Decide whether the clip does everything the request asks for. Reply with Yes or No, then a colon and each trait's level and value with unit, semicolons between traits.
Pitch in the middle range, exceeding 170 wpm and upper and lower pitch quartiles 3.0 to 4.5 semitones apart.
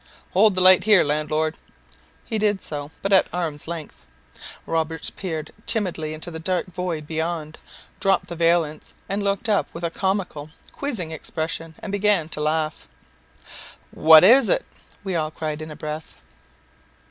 No: medium, 165 Hz; average, 155 wpm; average, 3.7 semitones